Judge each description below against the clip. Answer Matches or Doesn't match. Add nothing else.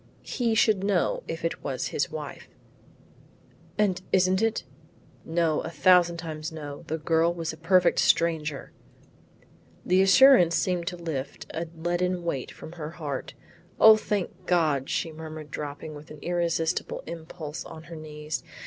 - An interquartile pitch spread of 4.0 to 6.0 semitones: Doesn't match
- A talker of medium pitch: Matches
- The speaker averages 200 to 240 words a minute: Doesn't match